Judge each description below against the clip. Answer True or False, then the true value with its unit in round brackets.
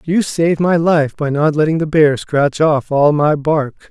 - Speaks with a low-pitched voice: False (155 Hz)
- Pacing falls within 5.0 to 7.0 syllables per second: False (4.2 syllables/s)